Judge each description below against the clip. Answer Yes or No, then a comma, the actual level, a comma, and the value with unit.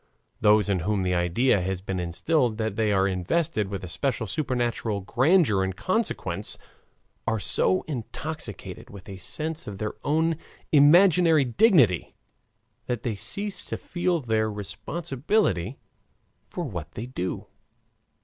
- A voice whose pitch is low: Yes, low, 110 Hz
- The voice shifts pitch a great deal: Yes, wide, 8.1 semitones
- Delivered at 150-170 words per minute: No, slow, 135 wpm